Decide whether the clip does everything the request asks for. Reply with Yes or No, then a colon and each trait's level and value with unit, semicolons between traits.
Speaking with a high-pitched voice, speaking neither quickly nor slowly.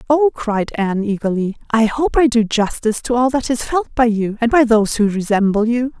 No: high, 230 Hz; fast, 220 wpm